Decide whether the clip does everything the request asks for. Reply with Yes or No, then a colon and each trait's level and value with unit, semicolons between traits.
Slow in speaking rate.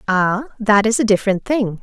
No: average, 195 wpm